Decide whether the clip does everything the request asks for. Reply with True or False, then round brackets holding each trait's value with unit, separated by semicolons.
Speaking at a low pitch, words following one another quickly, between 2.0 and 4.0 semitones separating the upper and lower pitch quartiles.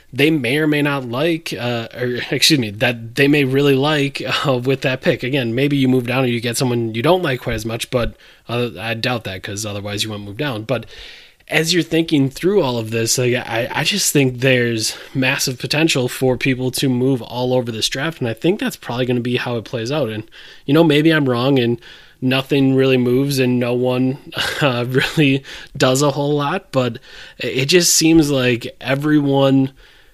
True (130 Hz; 210 wpm; 3.1 semitones)